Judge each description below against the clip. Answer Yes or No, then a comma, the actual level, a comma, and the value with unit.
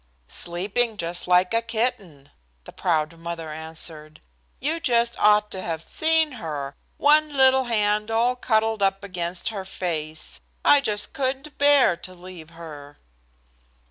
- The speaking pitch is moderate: No, high, 195 Hz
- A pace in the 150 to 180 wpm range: No, average, 140 wpm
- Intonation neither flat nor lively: No, wide, 6.5 semitones